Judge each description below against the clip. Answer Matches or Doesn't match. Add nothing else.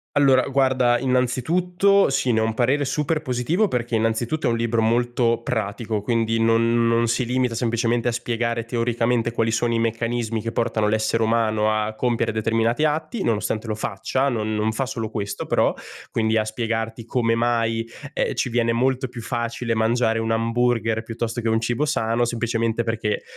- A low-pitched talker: Matches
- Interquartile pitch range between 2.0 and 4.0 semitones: Doesn't match